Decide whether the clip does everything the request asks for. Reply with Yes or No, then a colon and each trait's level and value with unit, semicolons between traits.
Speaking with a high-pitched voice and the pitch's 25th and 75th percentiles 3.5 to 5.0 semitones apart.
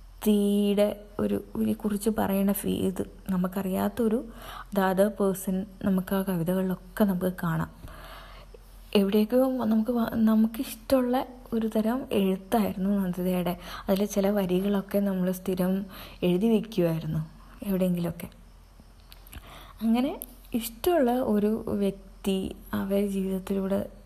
No: high, 200 Hz; average, 2.8 semitones